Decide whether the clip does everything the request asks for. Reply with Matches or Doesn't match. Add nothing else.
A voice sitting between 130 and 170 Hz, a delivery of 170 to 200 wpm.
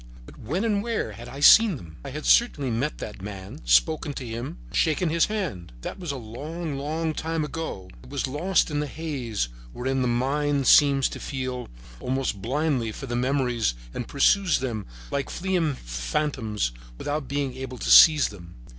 Matches